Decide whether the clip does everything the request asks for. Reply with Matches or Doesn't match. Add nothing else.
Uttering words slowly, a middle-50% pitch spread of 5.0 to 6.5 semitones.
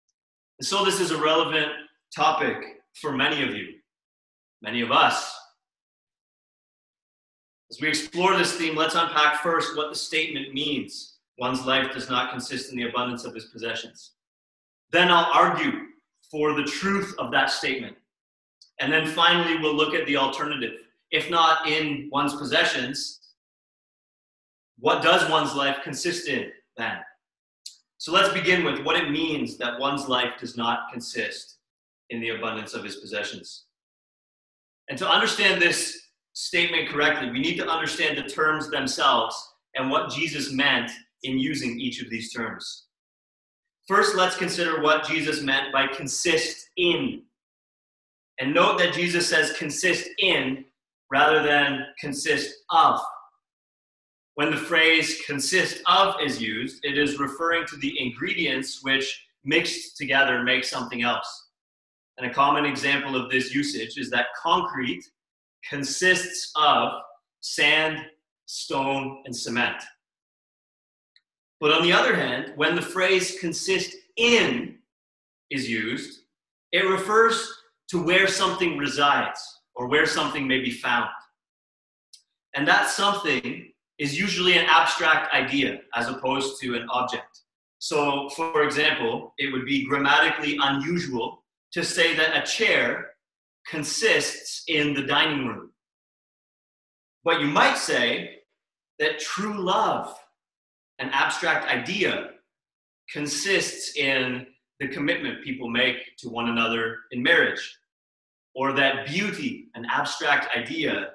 Doesn't match